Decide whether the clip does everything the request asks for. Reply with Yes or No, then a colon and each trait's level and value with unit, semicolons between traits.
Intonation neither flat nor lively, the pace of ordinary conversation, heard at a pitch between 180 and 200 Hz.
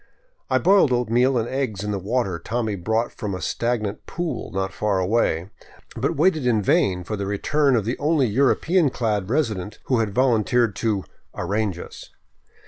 No: average, 4.3 semitones; average, 180 wpm; low, 115 Hz